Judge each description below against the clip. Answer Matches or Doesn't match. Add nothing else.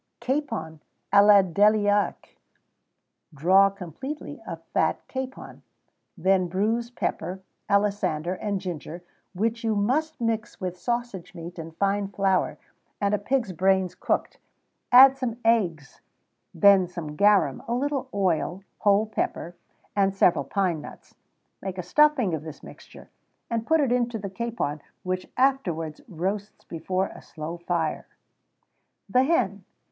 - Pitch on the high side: Matches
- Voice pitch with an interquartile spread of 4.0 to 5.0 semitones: Matches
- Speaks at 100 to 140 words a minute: Matches